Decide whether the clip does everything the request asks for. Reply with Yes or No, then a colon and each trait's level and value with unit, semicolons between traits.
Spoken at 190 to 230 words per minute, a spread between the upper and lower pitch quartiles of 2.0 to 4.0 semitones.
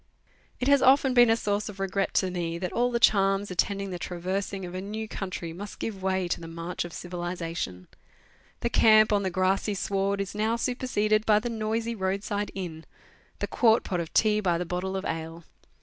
Yes: fast, 205 wpm; average, 3.2 semitones